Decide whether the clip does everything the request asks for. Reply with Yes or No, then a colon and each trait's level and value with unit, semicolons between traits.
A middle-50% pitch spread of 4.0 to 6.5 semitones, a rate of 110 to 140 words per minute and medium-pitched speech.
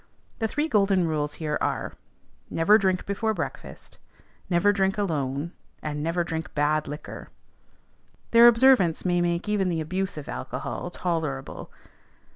Yes: average, 4.6 semitones; slow, 135 wpm; medium, 175 Hz